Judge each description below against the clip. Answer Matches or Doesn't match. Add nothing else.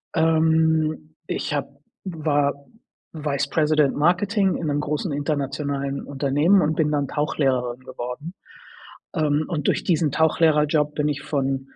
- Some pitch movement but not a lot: Doesn't match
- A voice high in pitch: Doesn't match